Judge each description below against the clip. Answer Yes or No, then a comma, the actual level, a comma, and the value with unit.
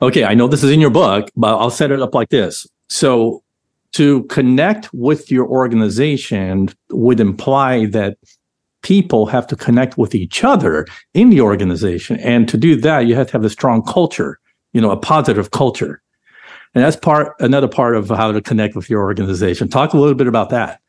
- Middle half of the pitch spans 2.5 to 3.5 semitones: No, average, 4.3 semitones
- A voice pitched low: Yes, low, 125 Hz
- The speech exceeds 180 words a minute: Yes, average, 195 wpm